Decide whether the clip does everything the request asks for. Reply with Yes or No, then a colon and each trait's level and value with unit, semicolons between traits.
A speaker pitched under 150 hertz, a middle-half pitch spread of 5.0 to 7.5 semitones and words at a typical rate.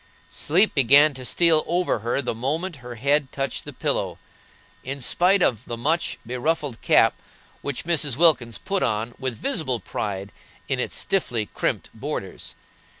Yes: medium, 140 Hz; average, 5.3 semitones; average, 150 wpm